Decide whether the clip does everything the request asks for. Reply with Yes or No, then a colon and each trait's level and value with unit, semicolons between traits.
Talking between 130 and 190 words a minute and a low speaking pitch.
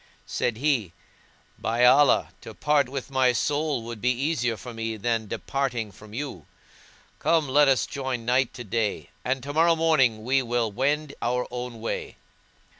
Yes: average, 165 wpm; low, 125 Hz